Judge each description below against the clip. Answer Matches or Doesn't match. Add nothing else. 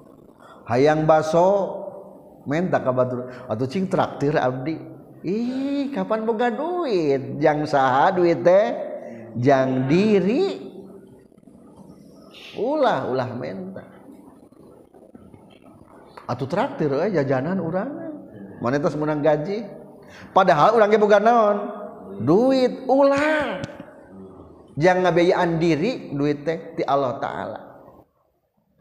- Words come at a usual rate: Doesn't match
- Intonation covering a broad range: Matches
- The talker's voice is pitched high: Doesn't match